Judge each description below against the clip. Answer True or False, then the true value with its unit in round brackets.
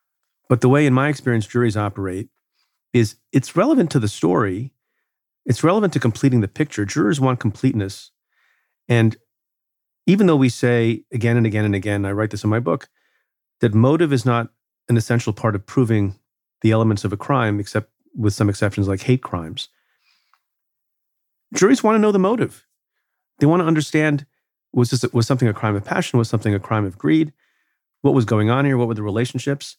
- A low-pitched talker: True (120 Hz)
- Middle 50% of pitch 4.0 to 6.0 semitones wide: True (4.3 semitones)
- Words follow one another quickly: False (190 wpm)